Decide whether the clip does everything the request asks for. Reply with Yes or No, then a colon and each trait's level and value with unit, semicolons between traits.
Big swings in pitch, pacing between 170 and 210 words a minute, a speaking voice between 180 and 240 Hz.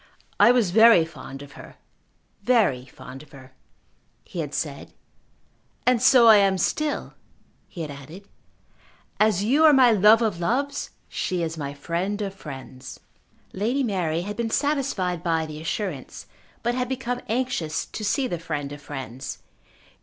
No: wide, 7.6 semitones; average, 155 wpm; high, 190 Hz